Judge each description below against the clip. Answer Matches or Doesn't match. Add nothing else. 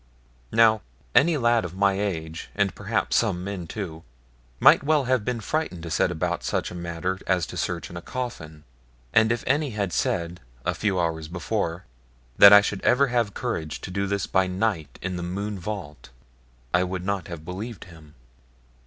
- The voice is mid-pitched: Doesn't match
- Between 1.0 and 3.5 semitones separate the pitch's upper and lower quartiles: Doesn't match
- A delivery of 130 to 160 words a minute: Doesn't match